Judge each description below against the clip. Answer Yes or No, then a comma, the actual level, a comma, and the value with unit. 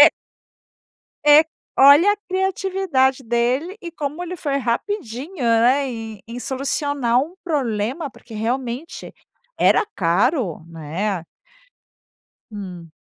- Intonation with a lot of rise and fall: Yes, wide, 6.1 semitones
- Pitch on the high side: Yes, very high, 260 Hz